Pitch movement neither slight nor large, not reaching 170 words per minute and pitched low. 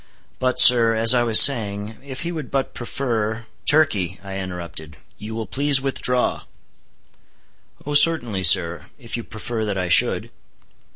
Yes: average, 4.8 semitones; average, 150 wpm; low, 115 Hz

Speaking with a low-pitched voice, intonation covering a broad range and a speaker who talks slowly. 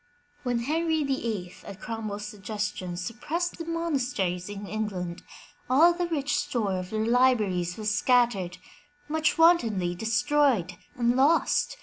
No: high, 230 Hz; wide, 7.0 semitones; slow, 125 wpm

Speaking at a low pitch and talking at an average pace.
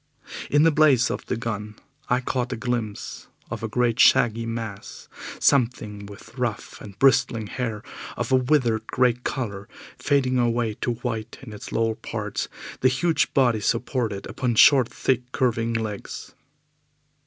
Yes: low, 120 Hz; average, 150 wpm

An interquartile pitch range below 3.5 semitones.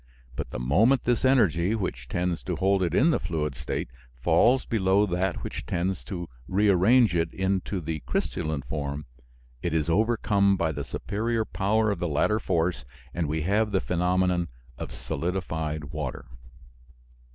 No: average, 4.3 semitones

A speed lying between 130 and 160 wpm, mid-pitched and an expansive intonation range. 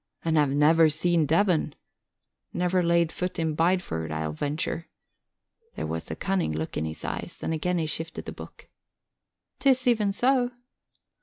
No: average, 155 wpm; medium, 165 Hz; average, 3.5 semitones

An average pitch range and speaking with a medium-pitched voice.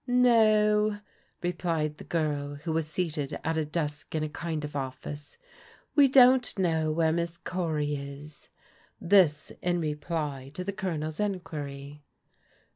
Yes: average, 3.5 semitones; medium, 160 Hz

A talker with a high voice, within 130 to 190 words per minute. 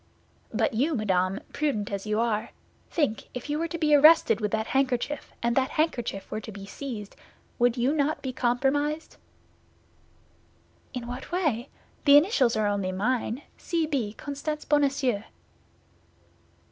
Yes: very high, 255 Hz; average, 145 wpm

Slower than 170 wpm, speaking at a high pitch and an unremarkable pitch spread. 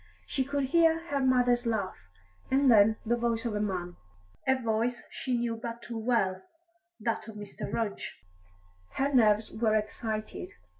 Yes: average, 155 wpm; high, 230 Hz; average, 3.0 semitones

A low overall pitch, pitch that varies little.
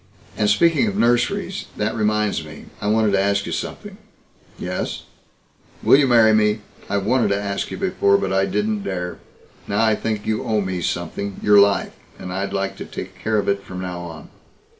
Yes: low, 100 Hz; narrow, 2.2 semitones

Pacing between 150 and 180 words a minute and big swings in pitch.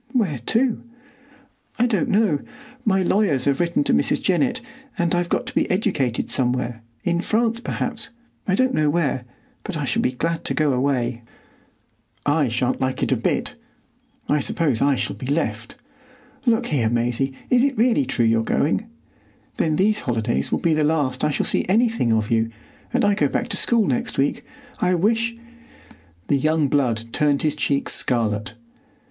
Yes: average, 170 wpm; wide, 8.0 semitones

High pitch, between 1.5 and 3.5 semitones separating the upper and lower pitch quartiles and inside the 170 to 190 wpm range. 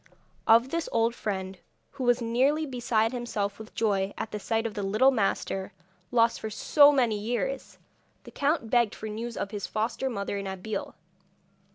Yes: high, 225 Hz; average, 3.0 semitones; average, 175 wpm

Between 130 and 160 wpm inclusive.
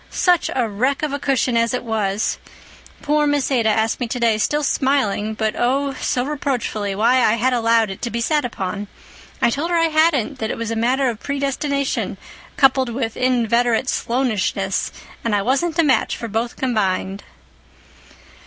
No: average, 170 wpm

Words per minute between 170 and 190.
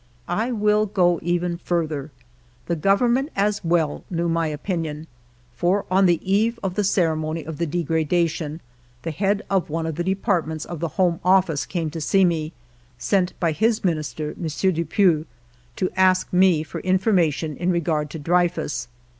No: average, 160 wpm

